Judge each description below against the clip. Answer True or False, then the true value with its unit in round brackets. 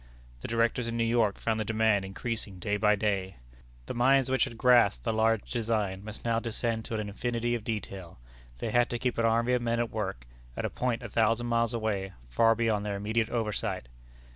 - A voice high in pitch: False (115 Hz)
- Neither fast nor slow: False (210 wpm)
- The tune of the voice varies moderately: False (2.1 semitones)